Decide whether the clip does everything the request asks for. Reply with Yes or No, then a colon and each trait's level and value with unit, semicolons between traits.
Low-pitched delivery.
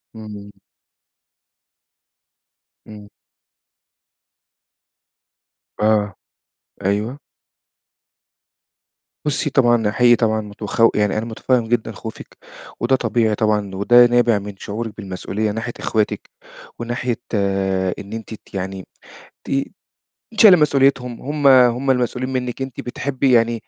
Yes: low, 115 Hz